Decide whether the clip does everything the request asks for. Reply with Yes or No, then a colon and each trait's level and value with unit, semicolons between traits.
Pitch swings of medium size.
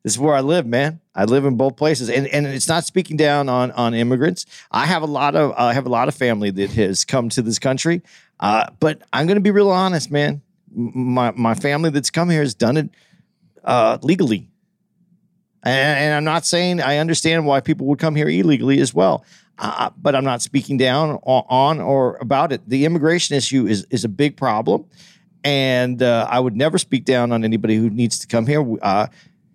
Yes: average, 4.3 semitones